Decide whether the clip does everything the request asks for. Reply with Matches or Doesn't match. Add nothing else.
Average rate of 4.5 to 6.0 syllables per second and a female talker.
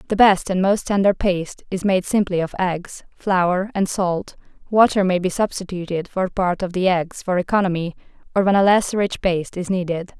Matches